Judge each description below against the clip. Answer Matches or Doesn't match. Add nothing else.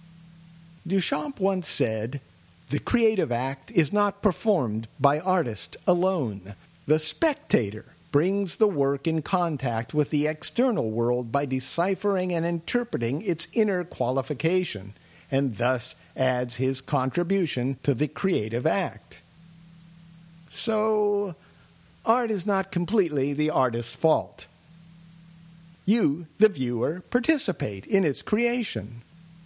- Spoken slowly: Matches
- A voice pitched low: Doesn't match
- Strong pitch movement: Matches